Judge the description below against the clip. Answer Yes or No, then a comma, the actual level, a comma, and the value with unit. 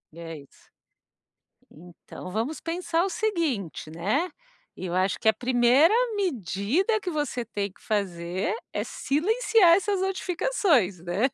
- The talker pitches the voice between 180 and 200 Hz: No, very high, 250 Hz